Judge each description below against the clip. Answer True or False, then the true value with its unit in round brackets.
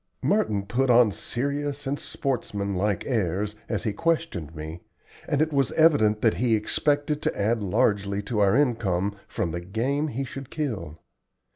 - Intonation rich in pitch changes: True (5.9 semitones)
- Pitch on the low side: True (110 Hz)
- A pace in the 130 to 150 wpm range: False (160 wpm)